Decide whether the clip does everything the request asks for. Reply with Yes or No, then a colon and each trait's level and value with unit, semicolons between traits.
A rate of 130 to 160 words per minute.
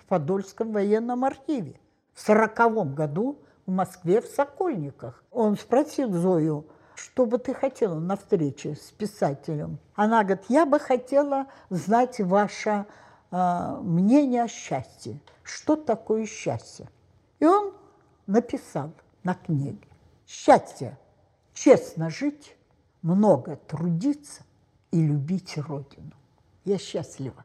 No: slow, 110 wpm